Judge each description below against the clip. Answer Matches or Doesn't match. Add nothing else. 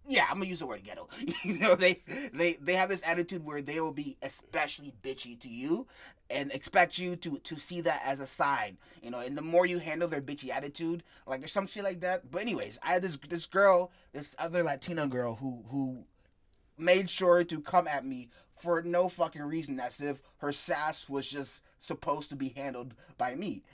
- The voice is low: Doesn't match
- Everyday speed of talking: Doesn't match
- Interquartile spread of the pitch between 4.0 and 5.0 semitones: Matches